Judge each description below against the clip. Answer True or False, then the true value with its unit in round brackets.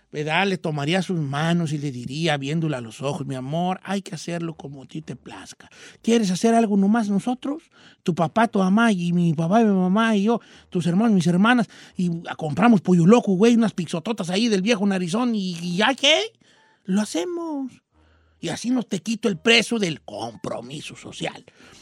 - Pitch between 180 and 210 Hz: True (190 Hz)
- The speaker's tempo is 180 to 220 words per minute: True (185 wpm)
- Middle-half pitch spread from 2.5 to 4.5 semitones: False (5.6 semitones)